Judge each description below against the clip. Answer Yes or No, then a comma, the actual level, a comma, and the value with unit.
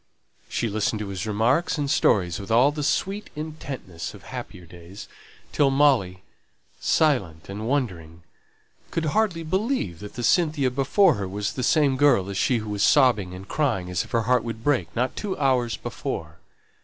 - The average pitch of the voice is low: Yes, low, 120 Hz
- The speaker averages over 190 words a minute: No, average, 175 wpm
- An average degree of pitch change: No, wide, 6.9 semitones